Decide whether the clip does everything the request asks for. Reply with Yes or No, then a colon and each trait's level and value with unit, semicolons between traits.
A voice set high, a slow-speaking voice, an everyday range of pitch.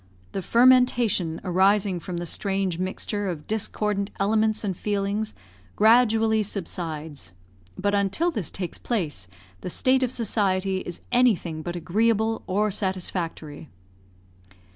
Yes: high, 200 Hz; slow, 120 wpm; average, 3.7 semitones